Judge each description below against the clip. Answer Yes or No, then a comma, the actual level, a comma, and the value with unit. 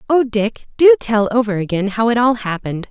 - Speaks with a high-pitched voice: Yes, high, 225 Hz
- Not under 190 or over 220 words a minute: Yes, fast, 205 wpm